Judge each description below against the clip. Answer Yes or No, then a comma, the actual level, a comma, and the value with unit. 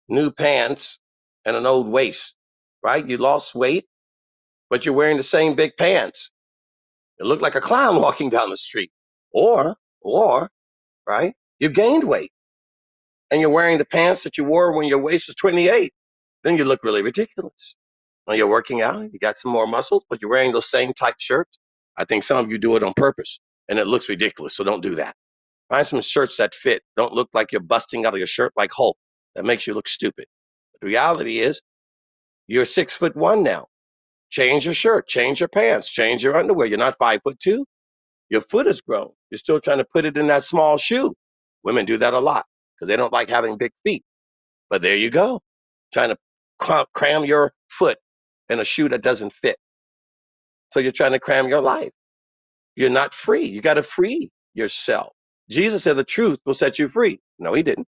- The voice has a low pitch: No, medium, 155 Hz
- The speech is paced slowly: No, average, 200 wpm